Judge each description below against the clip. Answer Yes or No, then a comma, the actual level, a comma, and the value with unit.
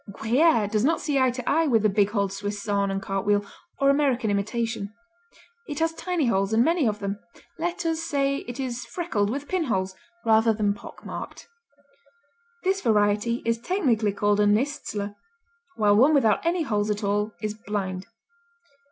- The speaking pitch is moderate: No, high, 220 Hz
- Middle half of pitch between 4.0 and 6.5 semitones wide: Yes, average, 5.3 semitones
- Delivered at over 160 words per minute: Yes, average, 170 wpm